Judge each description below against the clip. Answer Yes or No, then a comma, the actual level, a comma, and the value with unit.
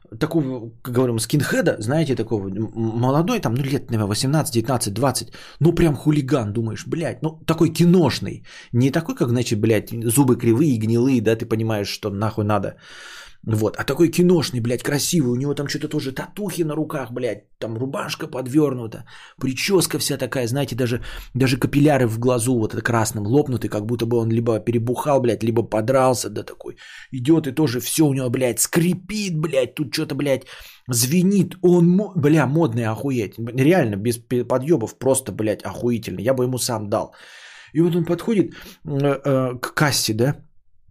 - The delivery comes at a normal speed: No, fast, 165 wpm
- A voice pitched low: Yes, low, 130 Hz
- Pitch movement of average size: Yes, average, 5.0 semitones